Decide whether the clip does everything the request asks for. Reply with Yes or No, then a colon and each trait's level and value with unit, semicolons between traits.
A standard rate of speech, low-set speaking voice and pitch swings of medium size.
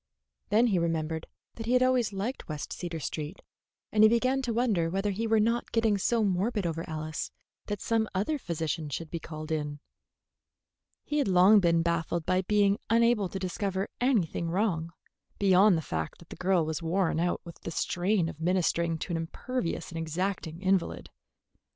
No: average, 180 wpm; medium, 185 Hz; average, 4.6 semitones